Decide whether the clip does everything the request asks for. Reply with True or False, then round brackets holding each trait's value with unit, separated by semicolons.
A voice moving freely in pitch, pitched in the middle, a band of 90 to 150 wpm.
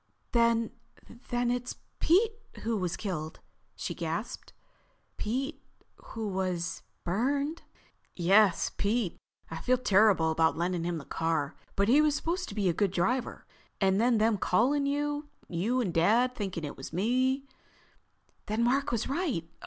False (6.0 semitones; 220 Hz; 140 wpm)